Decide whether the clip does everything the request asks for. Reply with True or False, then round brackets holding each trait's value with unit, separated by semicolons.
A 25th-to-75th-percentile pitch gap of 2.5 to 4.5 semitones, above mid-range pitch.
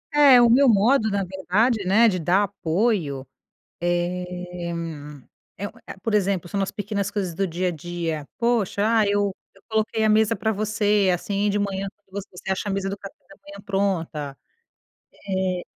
True (2.8 semitones; 195 Hz)